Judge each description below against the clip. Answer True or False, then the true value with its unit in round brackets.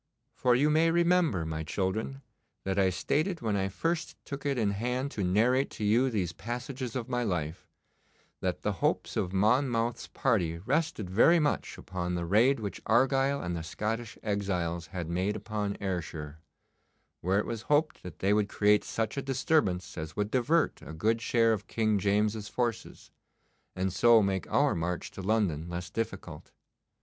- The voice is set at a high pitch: False (105 Hz)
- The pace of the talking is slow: False (170 wpm)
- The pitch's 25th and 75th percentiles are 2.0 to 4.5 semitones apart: False (5.2 semitones)